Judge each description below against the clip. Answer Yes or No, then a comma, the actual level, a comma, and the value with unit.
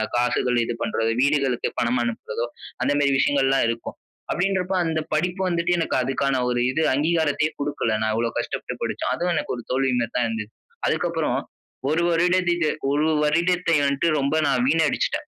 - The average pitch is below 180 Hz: Yes, medium, 140 Hz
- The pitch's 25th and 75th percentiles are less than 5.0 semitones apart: No, average, 5.3 semitones